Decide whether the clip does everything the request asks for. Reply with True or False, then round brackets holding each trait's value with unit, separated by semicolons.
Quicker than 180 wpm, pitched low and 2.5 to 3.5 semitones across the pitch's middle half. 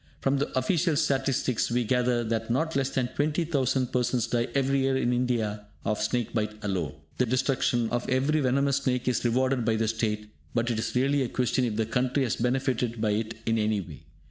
True (200 wpm; 125 Hz; 2.9 semitones)